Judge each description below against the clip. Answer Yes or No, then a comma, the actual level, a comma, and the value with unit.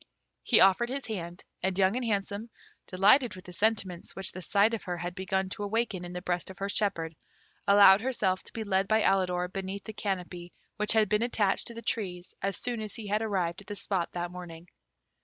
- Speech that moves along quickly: Yes, fast, 215 wpm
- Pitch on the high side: Yes, high, 195 Hz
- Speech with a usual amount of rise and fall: Yes, average, 3.0 semitones